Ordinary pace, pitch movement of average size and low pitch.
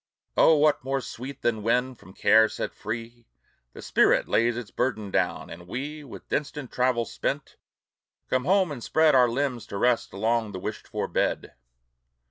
Yes: average, 170 wpm; average, 3.4 semitones; low, 120 Hz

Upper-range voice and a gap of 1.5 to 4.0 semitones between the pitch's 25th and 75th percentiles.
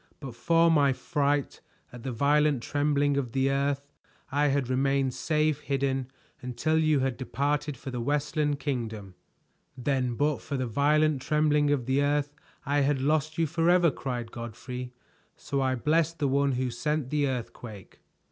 No: medium, 140 Hz; narrow, 2.4 semitones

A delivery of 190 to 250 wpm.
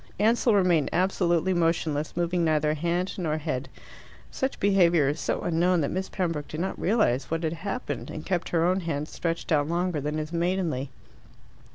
No: average, 175 wpm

